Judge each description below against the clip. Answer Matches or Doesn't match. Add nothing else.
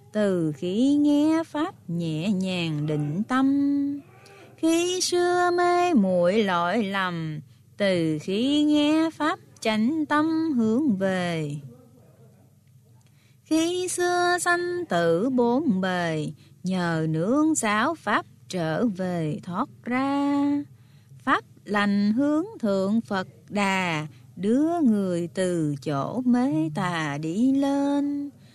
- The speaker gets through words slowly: Matches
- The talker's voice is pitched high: Matches